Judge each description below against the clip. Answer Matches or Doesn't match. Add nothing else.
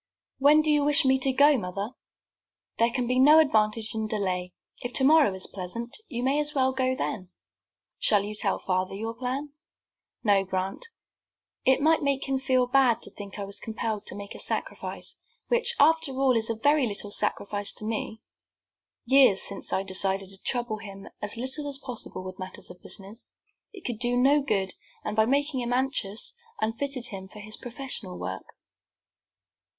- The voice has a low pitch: Doesn't match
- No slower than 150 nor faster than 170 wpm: Doesn't match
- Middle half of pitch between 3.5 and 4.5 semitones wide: Doesn't match